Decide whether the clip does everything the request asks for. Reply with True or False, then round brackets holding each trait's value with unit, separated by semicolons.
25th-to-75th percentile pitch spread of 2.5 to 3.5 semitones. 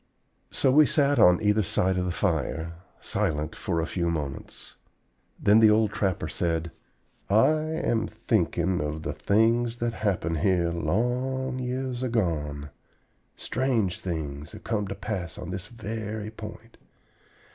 False (5.5 semitones)